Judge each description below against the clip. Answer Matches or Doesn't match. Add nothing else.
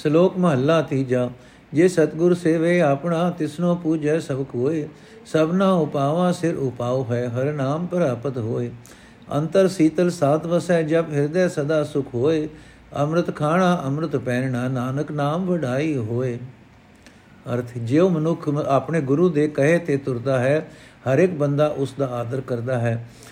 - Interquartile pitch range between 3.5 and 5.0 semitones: Matches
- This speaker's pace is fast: Doesn't match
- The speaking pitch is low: Doesn't match